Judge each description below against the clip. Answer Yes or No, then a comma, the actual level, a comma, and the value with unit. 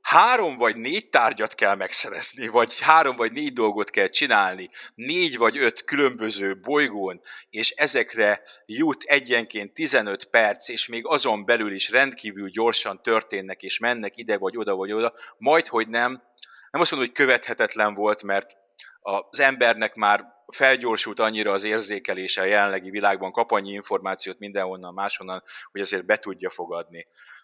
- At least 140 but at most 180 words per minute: Yes, average, 150 wpm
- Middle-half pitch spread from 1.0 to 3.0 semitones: No, average, 3.5 semitones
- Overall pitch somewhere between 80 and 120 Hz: Yes, low, 105 Hz